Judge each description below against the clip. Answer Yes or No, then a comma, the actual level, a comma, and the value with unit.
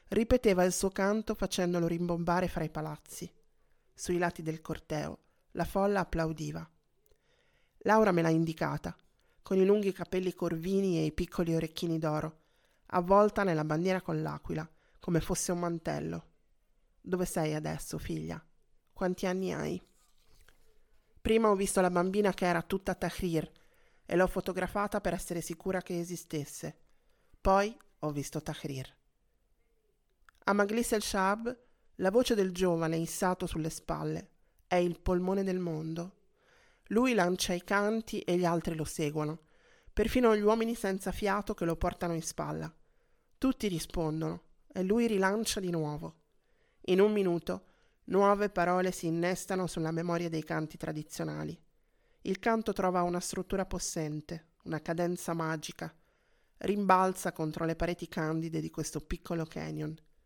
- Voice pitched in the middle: Yes, medium, 175 Hz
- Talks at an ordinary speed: Yes, average, 140 wpm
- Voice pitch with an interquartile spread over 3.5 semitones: No, average, 3.2 semitones